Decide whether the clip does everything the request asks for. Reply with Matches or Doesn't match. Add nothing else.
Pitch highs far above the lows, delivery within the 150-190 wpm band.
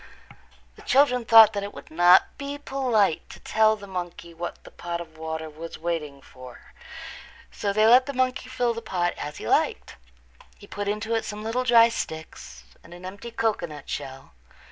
Matches